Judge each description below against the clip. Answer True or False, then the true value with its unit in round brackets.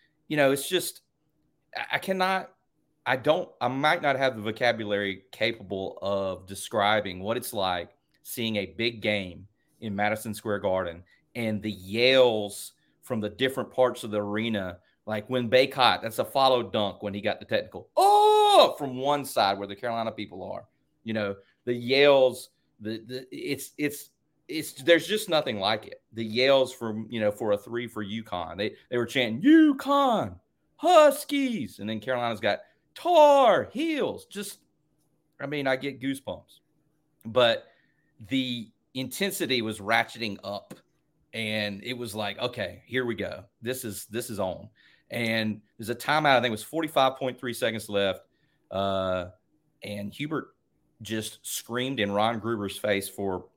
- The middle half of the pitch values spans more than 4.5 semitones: True (5.1 semitones)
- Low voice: True (120 Hz)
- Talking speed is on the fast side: False (160 wpm)